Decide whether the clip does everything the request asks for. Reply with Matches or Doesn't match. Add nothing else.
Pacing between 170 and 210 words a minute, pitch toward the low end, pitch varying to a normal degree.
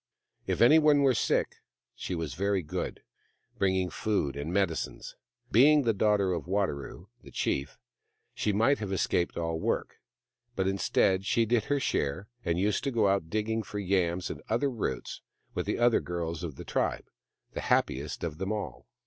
Matches